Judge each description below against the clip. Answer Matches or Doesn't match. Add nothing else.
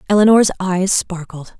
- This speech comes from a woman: Matches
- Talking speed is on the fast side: Doesn't match